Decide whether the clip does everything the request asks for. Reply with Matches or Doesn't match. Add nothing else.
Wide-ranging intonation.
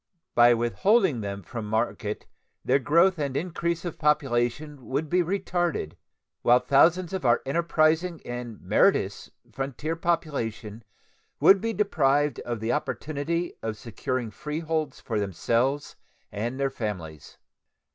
Matches